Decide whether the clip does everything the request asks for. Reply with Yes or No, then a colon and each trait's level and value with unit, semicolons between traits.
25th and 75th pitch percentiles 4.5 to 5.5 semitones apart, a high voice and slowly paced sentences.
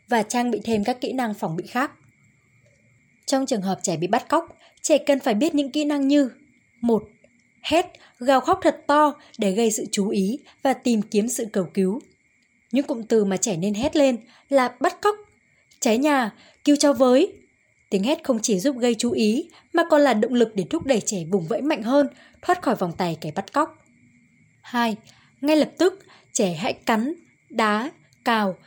No: average, 5.2 semitones; very high, 255 Hz; average, 200 wpm